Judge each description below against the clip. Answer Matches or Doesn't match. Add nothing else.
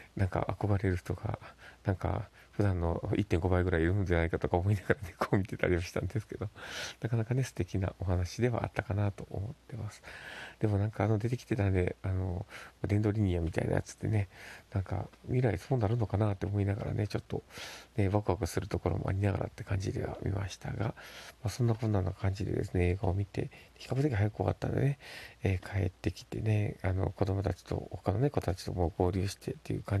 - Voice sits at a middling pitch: Doesn't match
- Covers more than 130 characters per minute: Matches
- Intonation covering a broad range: Doesn't match